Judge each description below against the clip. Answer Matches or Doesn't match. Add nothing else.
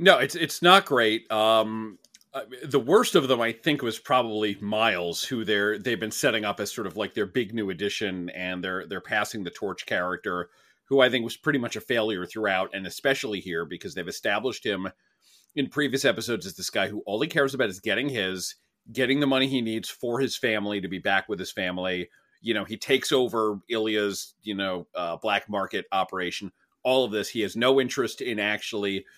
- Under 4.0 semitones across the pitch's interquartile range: Doesn't match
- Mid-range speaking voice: Doesn't match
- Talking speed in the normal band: Doesn't match